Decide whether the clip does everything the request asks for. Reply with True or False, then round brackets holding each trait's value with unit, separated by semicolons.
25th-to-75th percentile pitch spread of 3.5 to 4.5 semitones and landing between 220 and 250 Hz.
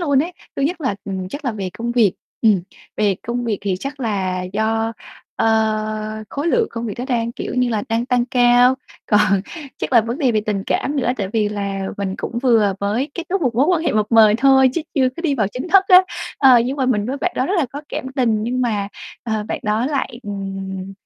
True (4.0 semitones; 230 Hz)